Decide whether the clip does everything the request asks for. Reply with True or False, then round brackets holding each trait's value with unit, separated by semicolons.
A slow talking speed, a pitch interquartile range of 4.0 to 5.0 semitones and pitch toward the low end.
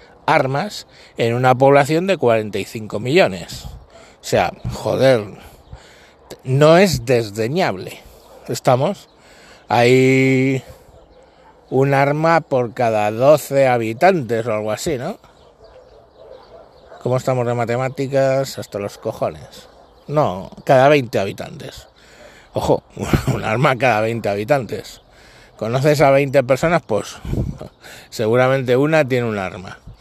False (105 wpm; 3.6 semitones; 130 Hz)